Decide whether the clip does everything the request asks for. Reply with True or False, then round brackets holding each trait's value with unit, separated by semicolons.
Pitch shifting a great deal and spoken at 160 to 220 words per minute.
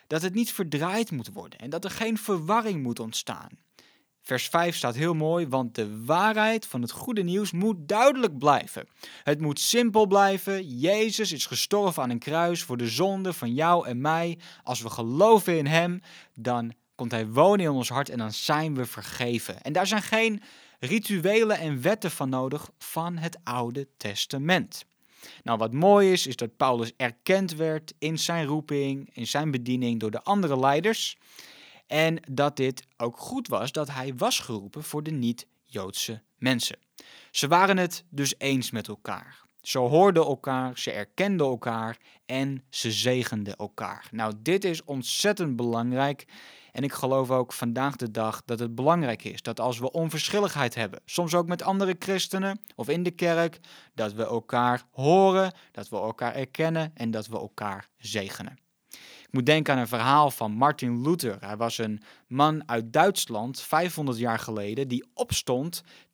True (6.7 semitones; 170 wpm)